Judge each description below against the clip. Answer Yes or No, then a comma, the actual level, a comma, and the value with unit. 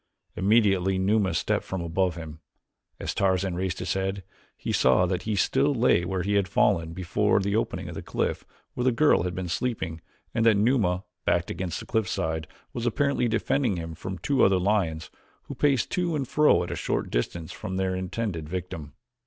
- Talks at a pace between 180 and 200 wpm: Yes, average, 185 wpm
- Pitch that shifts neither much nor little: Yes, average, 4.4 semitones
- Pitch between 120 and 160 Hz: No, very low, 95 Hz